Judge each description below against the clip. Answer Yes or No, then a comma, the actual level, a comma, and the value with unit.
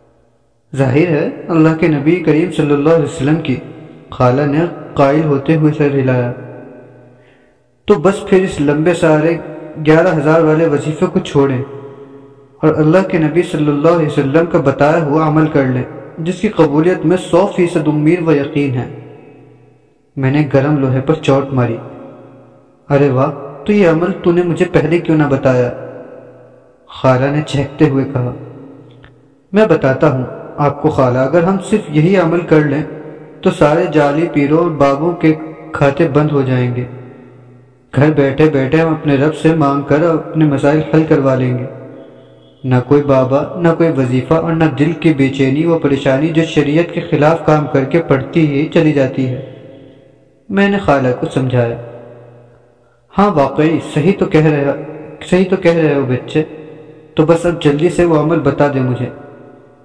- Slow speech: No, average, 170 wpm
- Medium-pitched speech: Yes, medium, 150 Hz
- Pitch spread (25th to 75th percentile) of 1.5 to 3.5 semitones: Yes, average, 2.9 semitones